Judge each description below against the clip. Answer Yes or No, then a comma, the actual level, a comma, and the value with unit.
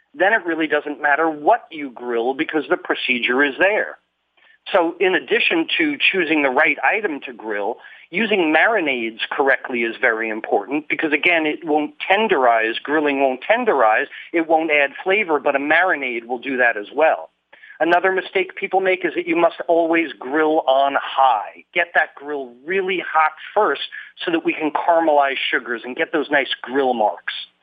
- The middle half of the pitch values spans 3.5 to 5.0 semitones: Yes, average, 4.4 semitones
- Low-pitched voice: No, medium, 155 Hz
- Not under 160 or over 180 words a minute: Yes, average, 170 wpm